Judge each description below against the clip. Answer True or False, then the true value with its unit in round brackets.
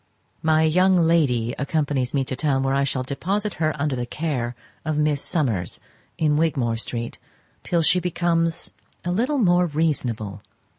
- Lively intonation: False (4.3 semitones)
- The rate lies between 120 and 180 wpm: True (155 wpm)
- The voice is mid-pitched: True (150 Hz)